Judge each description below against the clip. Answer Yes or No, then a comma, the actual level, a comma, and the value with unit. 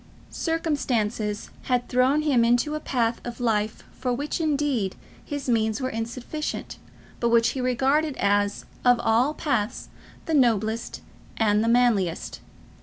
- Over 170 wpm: No, slow, 135 wpm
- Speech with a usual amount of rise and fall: Yes, average, 3.8 semitones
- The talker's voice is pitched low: No, high, 245 Hz